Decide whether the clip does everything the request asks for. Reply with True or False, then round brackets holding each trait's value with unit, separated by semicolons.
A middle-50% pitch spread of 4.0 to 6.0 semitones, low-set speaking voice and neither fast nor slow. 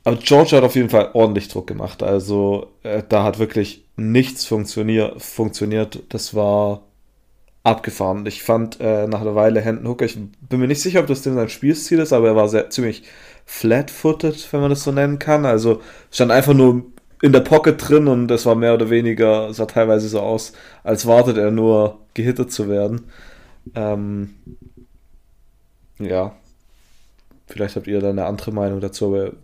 False (3.2 semitones; 110 Hz; 175 wpm)